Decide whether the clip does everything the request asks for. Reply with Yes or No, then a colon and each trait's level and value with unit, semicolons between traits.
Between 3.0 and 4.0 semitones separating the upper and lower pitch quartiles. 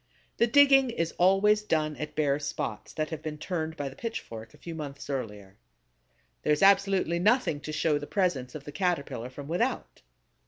No: average, 5.3 semitones